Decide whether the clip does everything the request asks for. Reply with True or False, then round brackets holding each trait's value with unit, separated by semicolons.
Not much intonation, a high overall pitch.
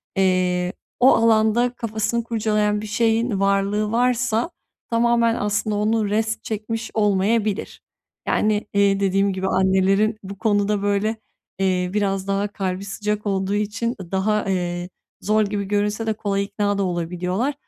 True (2.0 semitones; 205 Hz)